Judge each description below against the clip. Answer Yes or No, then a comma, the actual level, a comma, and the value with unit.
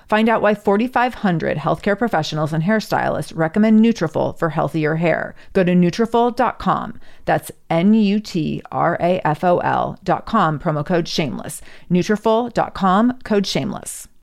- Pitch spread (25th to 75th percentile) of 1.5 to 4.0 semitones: No, average, 4.9 semitones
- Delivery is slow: Yes, slow, 100 wpm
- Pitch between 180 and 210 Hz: Yes, high, 190 Hz